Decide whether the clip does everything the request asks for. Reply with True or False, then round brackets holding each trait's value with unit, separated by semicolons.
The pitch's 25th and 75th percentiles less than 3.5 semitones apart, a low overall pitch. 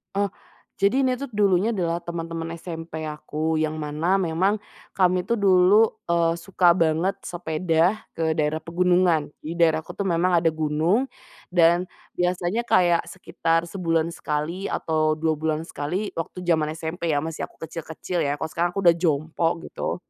False (2.4 semitones; 170 Hz)